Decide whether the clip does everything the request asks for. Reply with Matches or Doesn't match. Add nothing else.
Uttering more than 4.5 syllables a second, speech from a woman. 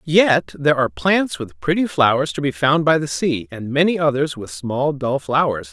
Doesn't match